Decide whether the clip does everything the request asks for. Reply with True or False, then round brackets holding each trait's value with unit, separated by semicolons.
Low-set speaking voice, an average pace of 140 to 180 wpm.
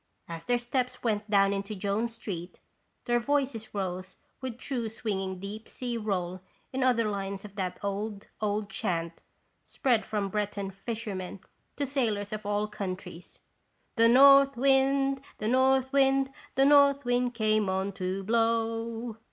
False (215 Hz; 150 wpm)